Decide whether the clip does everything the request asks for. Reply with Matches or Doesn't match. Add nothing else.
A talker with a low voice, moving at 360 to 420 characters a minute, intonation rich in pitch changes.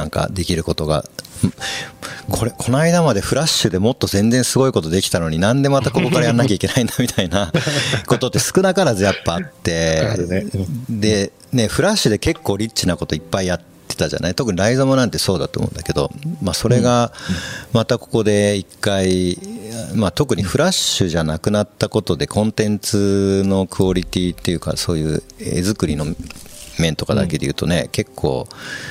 Matches